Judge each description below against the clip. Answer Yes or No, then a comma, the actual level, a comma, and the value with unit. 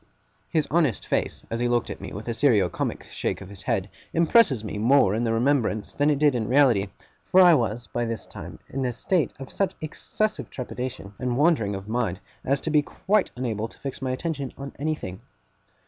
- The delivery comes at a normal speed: No, fast, 210 wpm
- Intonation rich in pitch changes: No, average, 4.7 semitones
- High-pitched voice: No, low, 125 Hz